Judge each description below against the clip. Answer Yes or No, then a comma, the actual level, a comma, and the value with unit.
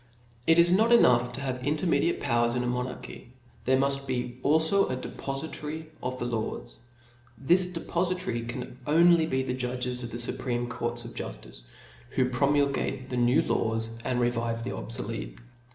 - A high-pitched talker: No, low, 130 Hz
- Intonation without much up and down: No, average, 3.7 semitones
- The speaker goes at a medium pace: Yes, average, 155 wpm